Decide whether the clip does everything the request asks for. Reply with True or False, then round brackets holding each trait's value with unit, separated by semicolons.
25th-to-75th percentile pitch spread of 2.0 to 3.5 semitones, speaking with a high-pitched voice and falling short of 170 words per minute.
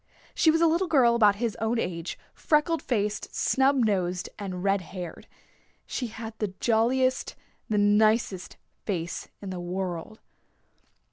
False (4.7 semitones; 215 Hz; 140 wpm)